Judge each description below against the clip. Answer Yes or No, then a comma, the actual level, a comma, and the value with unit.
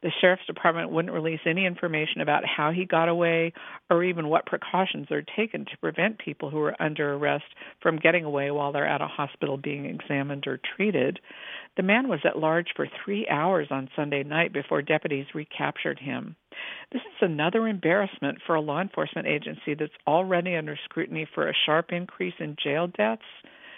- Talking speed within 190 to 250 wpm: No, average, 180 wpm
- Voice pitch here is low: No, medium, 165 Hz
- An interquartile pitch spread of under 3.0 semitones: No, average, 3.4 semitones